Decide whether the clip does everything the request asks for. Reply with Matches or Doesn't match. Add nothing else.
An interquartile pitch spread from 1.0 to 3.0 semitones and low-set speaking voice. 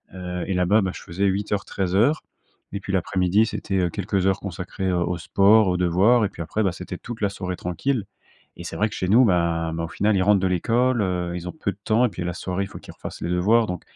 Matches